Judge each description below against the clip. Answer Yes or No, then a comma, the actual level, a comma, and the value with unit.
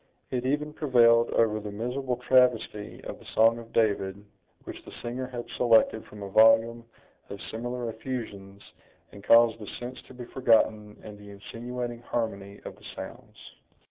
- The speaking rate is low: No, average, 160 wpm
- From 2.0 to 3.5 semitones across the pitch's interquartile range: Yes, average, 2.7 semitones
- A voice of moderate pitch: No, low, 115 Hz